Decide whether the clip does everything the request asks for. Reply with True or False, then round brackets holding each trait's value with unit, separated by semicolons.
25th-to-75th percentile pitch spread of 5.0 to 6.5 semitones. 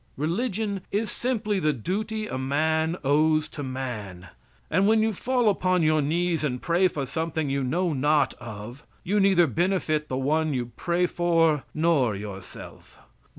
True (5.3 semitones)